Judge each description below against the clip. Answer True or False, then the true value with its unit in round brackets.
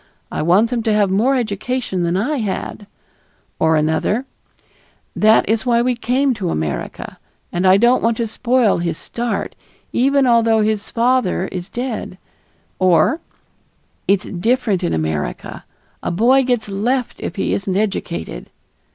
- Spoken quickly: False (145 wpm)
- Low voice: False (215 Hz)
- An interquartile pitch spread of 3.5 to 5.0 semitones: True (4.7 semitones)